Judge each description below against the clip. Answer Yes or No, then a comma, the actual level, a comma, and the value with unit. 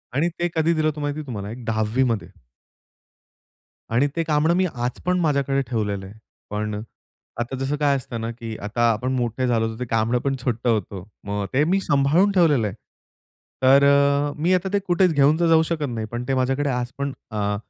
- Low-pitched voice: Yes, low, 130 Hz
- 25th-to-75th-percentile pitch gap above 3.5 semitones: Yes, average, 5.1 semitones